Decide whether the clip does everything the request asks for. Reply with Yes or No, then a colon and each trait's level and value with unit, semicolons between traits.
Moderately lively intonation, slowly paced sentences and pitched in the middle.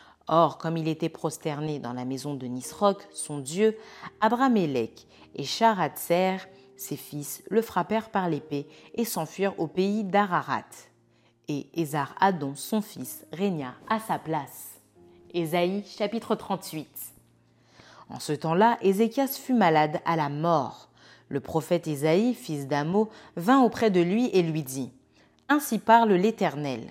No: wide, 6.2 semitones; slow, 135 wpm; medium, 165 Hz